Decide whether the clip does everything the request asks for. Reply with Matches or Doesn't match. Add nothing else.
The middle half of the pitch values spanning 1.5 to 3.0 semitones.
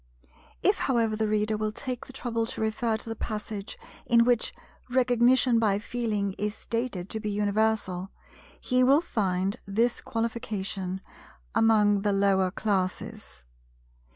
Matches